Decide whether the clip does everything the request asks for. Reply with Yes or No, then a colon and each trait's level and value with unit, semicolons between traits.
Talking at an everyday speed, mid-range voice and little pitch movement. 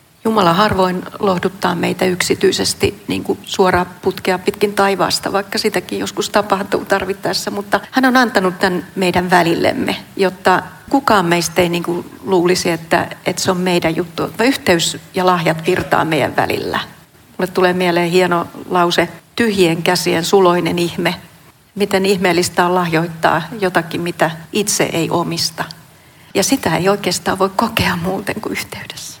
Yes: average, 140 wpm; medium, 180 Hz; narrow, 2.3 semitones